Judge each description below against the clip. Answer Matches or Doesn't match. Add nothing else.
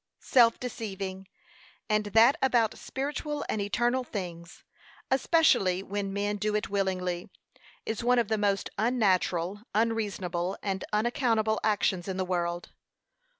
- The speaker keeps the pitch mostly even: Doesn't match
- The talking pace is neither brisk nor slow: Doesn't match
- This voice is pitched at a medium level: Doesn't match